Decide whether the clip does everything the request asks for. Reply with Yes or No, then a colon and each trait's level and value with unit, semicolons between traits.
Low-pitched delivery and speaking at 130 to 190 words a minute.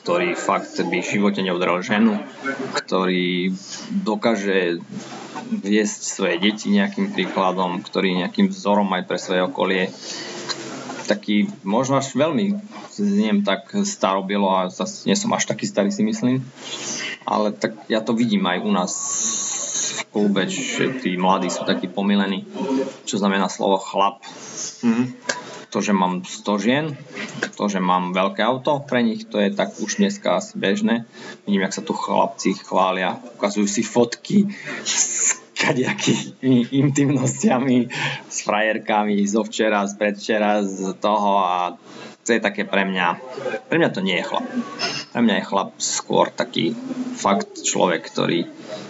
Yes: low, 105 Hz; average, 145 wpm